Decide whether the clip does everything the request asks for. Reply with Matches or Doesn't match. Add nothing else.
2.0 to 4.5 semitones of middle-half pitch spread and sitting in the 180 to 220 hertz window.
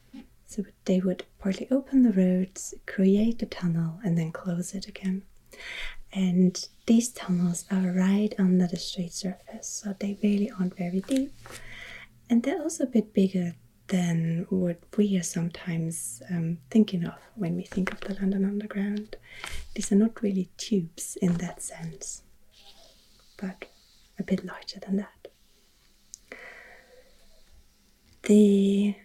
Matches